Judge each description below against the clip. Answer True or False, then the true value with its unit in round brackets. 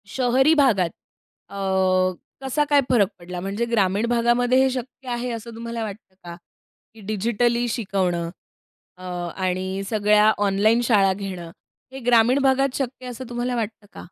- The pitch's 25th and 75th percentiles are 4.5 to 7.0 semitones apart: False (4.0 semitones)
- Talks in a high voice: True (225 Hz)